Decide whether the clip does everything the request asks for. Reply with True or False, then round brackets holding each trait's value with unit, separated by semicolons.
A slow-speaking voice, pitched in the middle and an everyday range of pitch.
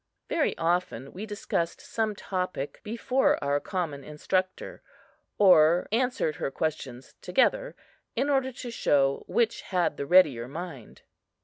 False (125 wpm; 180 Hz; 7.4 semitones)